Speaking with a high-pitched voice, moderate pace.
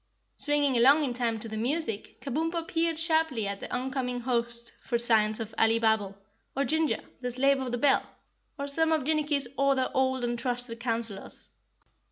Yes: very high, 255 Hz; average, 170 wpm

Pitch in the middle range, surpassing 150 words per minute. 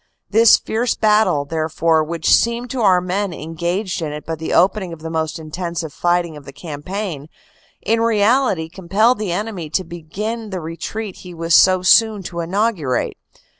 Yes: medium, 175 Hz; average, 170 wpm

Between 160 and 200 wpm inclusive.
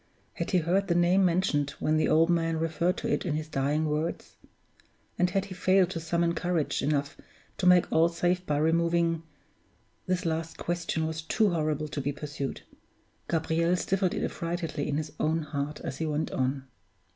Yes: average, 180 wpm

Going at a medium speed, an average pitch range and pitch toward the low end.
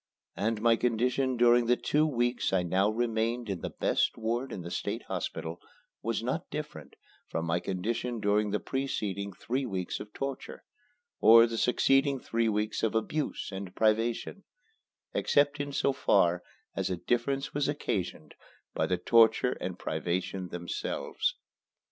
Yes: average, 150 wpm; average, 4.3 semitones; low, 115 Hz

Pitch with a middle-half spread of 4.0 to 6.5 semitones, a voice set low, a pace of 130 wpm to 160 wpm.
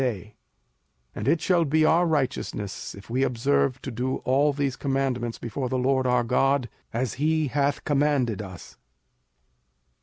No: average, 3.2 semitones; low, 130 Hz; average, 150 wpm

